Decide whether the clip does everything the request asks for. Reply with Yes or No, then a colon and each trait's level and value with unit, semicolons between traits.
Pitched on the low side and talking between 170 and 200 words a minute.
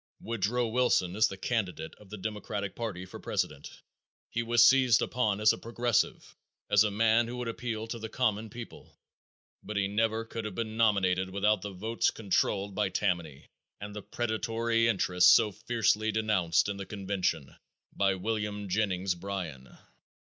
No: low, 105 Hz; average, 160 wpm